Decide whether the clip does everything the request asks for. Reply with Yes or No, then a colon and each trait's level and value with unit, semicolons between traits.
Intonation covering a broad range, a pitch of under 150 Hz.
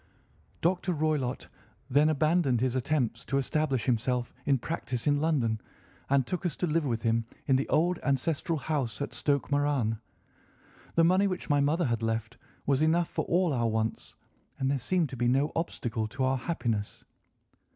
No: average, 4.5 semitones; medium, 140 Hz